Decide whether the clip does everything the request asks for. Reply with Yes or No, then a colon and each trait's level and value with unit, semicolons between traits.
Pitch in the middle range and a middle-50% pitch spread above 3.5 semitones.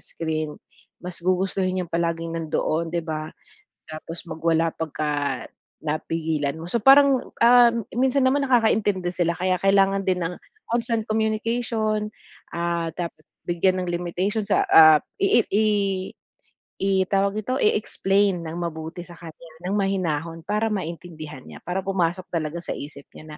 Yes: medium, 175 Hz; average, 4.0 semitones